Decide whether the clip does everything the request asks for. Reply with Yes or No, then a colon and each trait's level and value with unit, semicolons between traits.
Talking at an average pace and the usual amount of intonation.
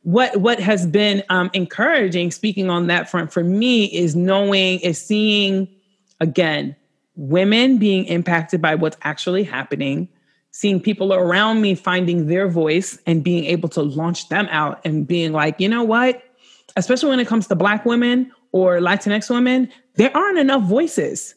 Yes: average, 165 wpm; average, 3.8 semitones